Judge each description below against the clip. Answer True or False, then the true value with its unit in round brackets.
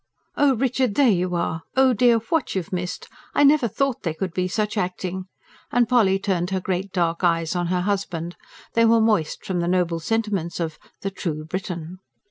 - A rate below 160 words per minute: False (190 wpm)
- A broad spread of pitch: False (4.4 semitones)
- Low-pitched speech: False (185 Hz)